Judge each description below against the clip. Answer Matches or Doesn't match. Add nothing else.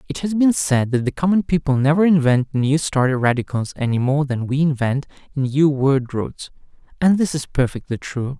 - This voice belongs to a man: Matches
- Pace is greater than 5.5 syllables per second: Doesn't match